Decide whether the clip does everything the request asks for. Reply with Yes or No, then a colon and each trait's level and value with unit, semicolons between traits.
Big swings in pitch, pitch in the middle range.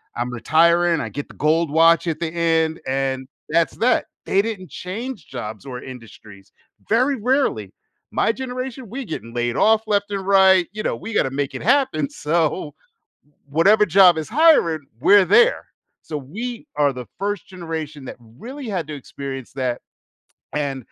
Yes: wide, 7.3 semitones; medium, 165 Hz